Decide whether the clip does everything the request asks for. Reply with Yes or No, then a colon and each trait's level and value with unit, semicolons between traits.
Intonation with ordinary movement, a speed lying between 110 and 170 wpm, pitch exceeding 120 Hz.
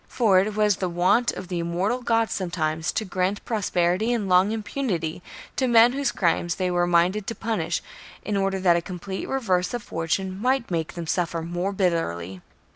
No: average, 3.9 semitones; average, 185 wpm; medium, 185 Hz